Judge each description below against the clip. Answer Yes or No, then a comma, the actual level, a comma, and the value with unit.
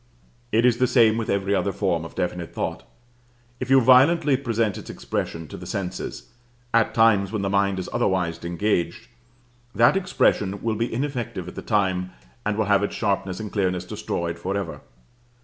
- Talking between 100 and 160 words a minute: No, average, 175 wpm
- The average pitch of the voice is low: Yes, low, 100 Hz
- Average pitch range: Yes, average, 4.0 semitones